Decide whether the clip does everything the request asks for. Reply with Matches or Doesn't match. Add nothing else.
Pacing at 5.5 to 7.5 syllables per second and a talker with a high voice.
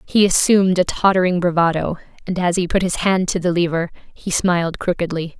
Doesn't match